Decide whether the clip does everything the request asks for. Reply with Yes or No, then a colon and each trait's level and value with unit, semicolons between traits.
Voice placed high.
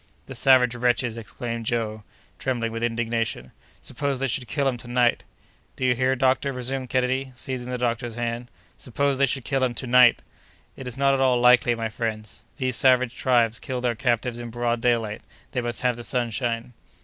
No: low, 125 Hz